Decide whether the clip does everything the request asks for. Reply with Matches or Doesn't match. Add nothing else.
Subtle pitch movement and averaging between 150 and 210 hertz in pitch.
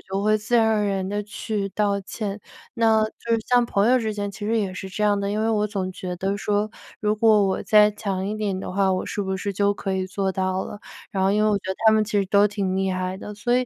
Matches